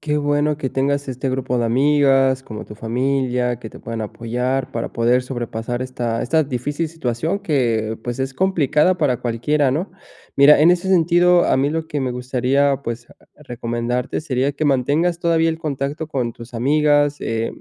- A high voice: No, low, 135 Hz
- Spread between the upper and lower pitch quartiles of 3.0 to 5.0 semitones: Yes, average, 3.5 semitones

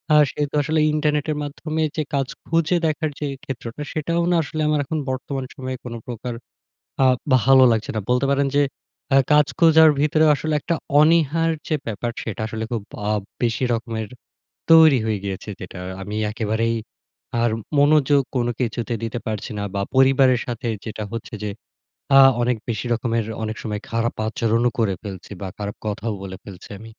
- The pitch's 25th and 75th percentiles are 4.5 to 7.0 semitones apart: Yes, average, 5.1 semitones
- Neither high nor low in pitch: No, low, 125 Hz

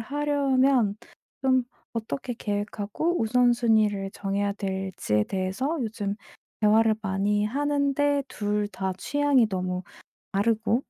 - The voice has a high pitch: Yes, high, 220 Hz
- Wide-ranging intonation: No, average, 4.8 semitones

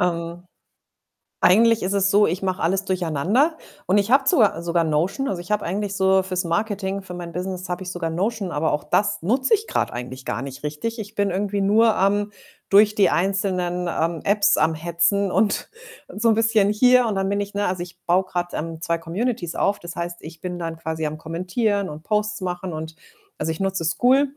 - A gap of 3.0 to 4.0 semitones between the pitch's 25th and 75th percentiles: Yes, average, 3.5 semitones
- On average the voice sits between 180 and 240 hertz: Yes, high, 190 Hz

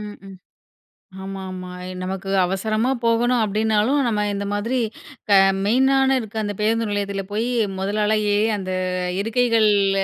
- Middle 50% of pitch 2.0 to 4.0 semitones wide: Yes, narrow, 2.5 semitones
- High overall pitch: Yes, high, 210 Hz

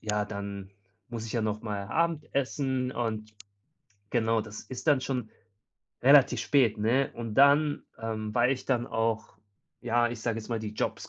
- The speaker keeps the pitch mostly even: No, average, 3.2 semitones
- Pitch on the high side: No, low, 115 Hz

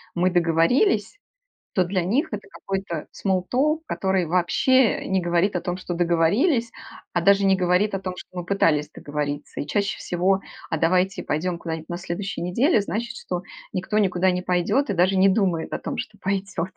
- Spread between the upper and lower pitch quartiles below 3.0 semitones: Yes, narrow, 2.5 semitones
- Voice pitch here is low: No, medium, 185 Hz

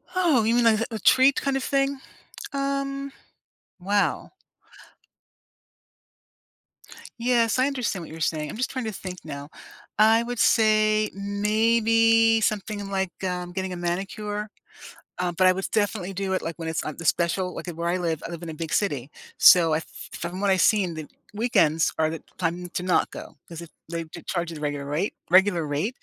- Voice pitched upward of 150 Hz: Yes, high, 190 Hz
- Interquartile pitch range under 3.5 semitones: No, average, 4.8 semitones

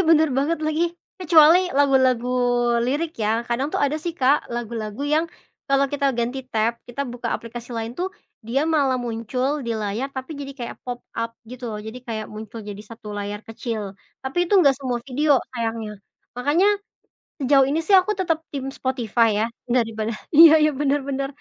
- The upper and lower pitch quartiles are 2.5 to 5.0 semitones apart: Yes, average, 3.9 semitones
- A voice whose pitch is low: No, very high, 255 Hz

